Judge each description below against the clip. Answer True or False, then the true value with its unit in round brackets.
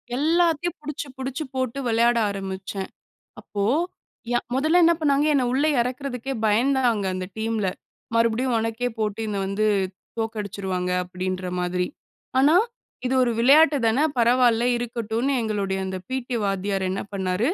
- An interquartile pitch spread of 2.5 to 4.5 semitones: False (4.9 semitones)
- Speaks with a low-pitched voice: False (230 Hz)